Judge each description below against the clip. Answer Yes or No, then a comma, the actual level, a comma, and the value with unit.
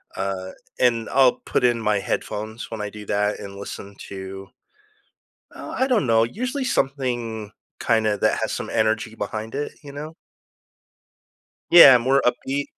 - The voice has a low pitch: Yes, low, 115 Hz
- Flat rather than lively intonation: No, average, 4.5 semitones